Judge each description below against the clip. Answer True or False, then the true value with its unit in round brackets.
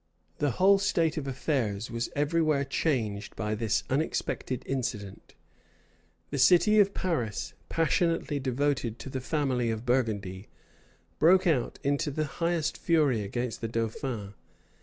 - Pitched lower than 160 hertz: True (135 Hz)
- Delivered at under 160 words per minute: True (135 wpm)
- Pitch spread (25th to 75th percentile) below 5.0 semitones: False (5.5 semitones)